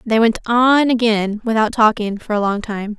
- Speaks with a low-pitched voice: No, high, 220 Hz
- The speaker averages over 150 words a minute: Yes, average, 200 wpm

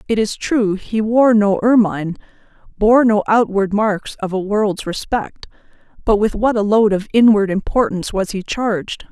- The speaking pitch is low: No, high, 210 Hz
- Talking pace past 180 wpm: No, average, 170 wpm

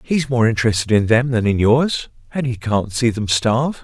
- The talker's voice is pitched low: Yes, low, 120 Hz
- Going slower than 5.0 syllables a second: No, 5.1 syllables/s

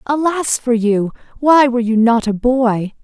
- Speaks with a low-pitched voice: No, high, 245 Hz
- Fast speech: No, average, 180 wpm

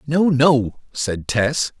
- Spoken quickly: No, slow, 135 wpm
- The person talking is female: No, male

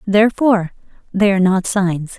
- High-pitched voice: Yes, high, 195 Hz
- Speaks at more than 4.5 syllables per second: Yes, 5.4 syllables/s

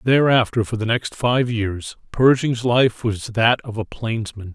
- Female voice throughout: No, male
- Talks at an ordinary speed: Yes, average, 170 wpm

